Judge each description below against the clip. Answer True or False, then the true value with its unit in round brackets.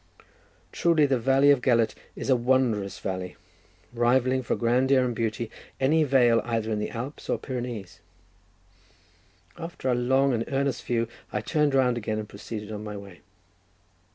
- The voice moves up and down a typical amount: True (3.2 semitones)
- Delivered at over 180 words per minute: False (155 wpm)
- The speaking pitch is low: True (120 Hz)